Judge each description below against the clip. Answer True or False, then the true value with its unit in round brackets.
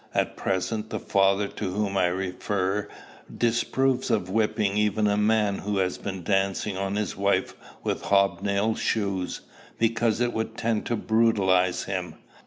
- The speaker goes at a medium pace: True (155 wpm)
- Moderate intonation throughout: False (2.3 semitones)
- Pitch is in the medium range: False (100 Hz)